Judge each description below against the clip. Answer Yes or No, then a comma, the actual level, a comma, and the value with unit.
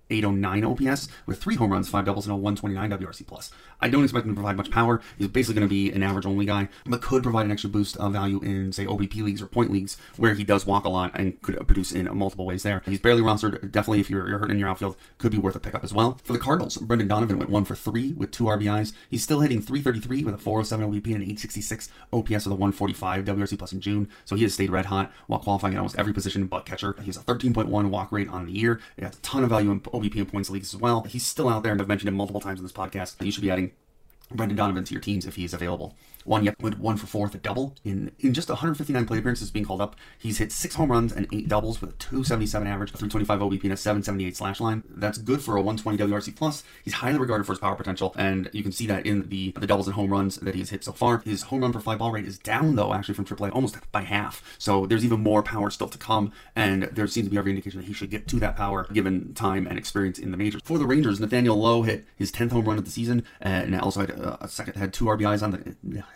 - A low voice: Yes, low, 105 Hz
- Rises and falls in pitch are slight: Yes, narrow, 2.3 semitones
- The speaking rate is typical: No, fast, 275 wpm